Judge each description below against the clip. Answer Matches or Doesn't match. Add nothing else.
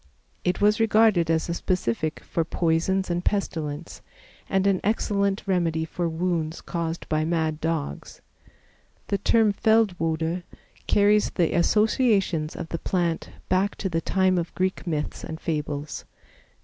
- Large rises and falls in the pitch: Doesn't match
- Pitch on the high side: Doesn't match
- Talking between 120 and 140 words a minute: Matches